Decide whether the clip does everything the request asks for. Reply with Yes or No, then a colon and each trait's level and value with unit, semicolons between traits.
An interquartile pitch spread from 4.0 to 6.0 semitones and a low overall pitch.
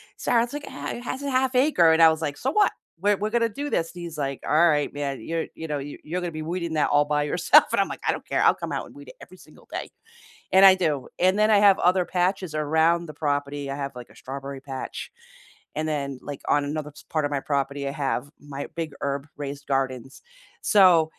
No: average, 4.3 semitones; medium, 155 Hz